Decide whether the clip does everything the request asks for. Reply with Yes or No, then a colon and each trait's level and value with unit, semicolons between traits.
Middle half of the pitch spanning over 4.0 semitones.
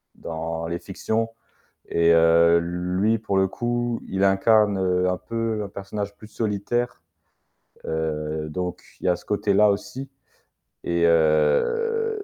Yes: average, 4.7 semitones